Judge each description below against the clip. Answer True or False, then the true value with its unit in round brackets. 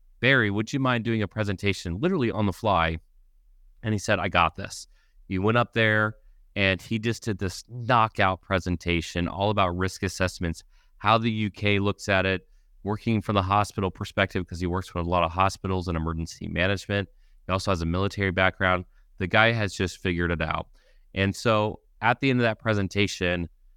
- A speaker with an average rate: True (190 wpm)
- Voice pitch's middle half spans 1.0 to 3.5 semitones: True (3.2 semitones)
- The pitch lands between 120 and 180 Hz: False (95 Hz)